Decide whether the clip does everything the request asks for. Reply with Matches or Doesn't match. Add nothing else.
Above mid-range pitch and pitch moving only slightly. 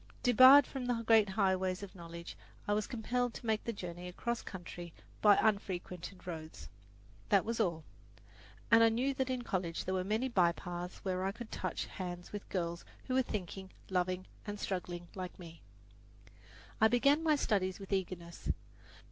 Doesn't match